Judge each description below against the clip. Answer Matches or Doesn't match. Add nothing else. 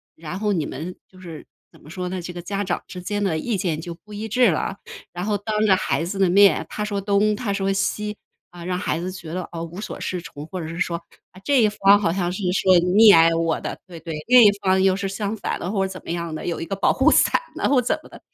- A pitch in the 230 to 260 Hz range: Doesn't match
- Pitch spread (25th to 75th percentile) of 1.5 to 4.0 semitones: Matches